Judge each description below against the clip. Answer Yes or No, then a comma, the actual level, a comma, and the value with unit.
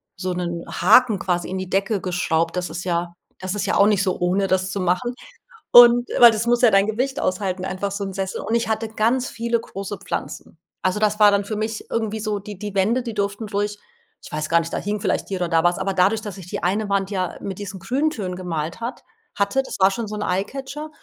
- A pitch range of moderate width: Yes, average, 3.1 semitones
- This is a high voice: Yes, high, 200 Hz